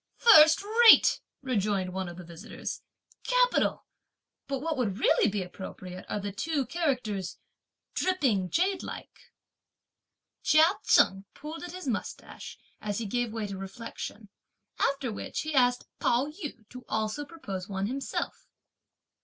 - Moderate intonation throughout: No, wide, 7.6 semitones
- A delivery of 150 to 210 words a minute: No, slow, 135 wpm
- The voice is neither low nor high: No, high, 245 Hz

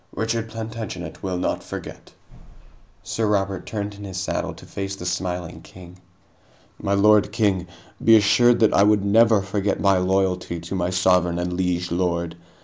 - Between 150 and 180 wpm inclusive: Yes, average, 160 wpm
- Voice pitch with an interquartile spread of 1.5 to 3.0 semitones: Yes, average, 2.7 semitones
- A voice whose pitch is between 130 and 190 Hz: No, very low, 95 Hz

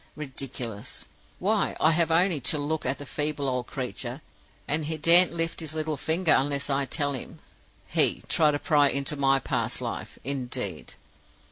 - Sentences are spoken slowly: No, average, 165 wpm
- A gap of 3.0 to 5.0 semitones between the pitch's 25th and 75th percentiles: No, narrow, 2.6 semitones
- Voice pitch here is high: No, medium, 145 Hz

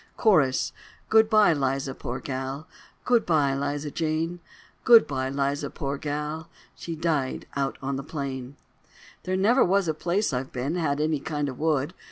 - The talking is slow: No, average, 145 wpm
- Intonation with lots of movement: No, average, 3.6 semitones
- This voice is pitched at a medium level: Yes, medium, 150 Hz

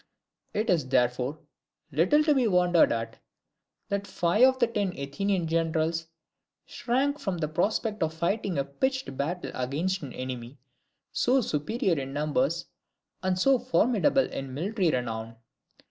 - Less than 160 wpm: Yes, average, 140 wpm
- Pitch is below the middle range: No, medium, 175 Hz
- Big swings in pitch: Yes, wide, 7.9 semitones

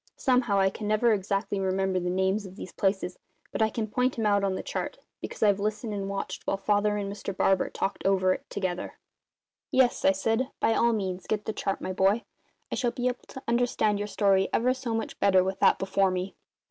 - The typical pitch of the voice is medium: No, high, 200 Hz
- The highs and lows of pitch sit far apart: No, average, 2.7 semitones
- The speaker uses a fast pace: Yes, fast, 220 wpm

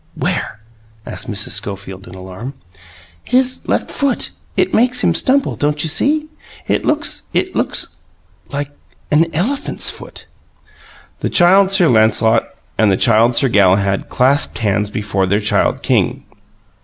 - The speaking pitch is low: Yes, low, 120 Hz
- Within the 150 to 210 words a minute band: No, average, 140 wpm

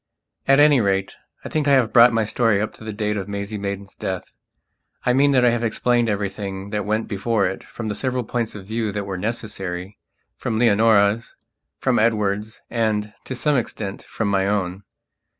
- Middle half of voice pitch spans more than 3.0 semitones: No, average, 2.7 semitones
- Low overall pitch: Yes, low, 110 Hz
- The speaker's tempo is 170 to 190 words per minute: Yes, average, 185 wpm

